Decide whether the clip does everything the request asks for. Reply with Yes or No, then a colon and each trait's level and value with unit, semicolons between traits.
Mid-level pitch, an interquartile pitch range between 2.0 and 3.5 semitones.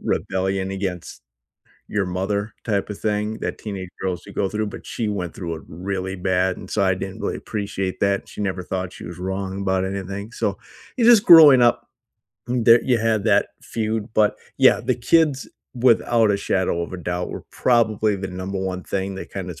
No: low, 100 Hz; narrow, 2.6 semitones